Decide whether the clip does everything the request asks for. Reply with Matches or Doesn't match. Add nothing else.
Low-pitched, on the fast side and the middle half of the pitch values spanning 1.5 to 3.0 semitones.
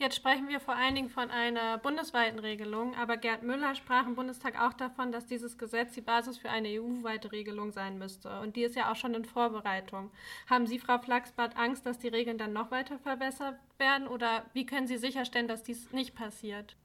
Doesn't match